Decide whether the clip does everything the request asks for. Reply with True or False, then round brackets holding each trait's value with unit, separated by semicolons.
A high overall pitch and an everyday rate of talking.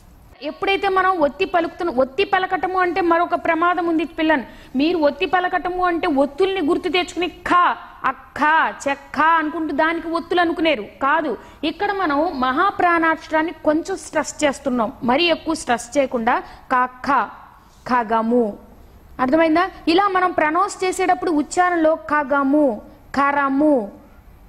True (325 Hz; 115 wpm)